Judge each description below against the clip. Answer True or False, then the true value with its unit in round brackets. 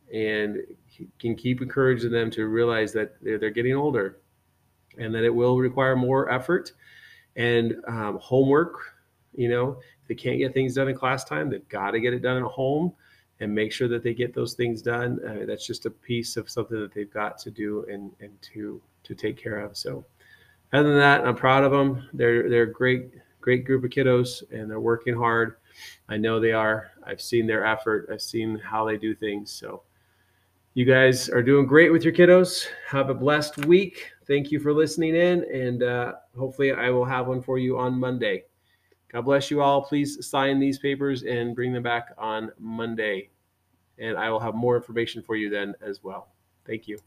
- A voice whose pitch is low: True (120 Hz)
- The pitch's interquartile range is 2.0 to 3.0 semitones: False (3.5 semitones)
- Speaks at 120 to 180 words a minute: False (200 wpm)